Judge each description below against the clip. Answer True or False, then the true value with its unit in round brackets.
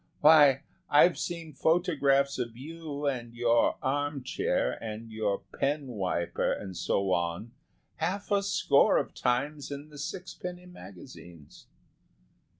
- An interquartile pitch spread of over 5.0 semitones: True (5.5 semitones)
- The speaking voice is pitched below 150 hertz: True (140 Hz)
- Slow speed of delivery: True (125 wpm)